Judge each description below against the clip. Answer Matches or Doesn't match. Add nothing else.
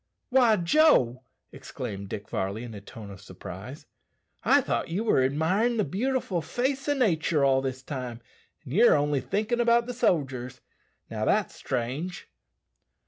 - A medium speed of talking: Matches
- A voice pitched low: Doesn't match